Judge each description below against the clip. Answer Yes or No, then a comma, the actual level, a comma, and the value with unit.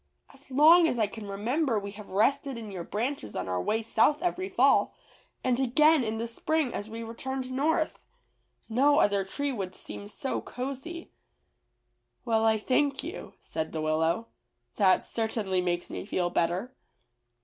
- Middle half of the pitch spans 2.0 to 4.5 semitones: No, wide, 5.6 semitones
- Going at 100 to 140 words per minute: No, average, 160 wpm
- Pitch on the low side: No, high, 230 Hz